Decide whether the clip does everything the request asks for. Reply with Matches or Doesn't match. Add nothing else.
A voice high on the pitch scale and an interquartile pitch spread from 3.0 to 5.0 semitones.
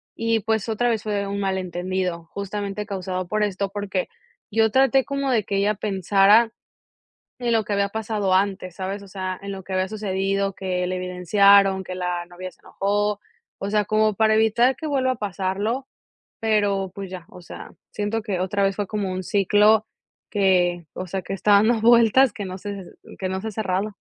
Doesn't match